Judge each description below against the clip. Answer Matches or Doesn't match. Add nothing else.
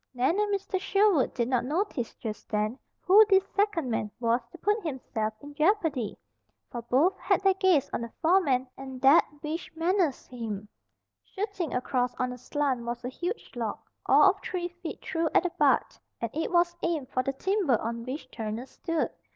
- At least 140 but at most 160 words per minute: Doesn't match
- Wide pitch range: Matches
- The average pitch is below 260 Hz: Doesn't match